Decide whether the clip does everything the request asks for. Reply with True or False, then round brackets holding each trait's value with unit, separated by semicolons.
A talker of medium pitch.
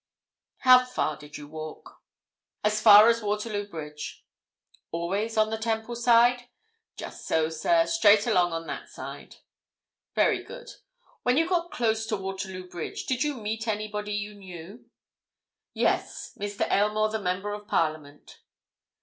False (210 Hz)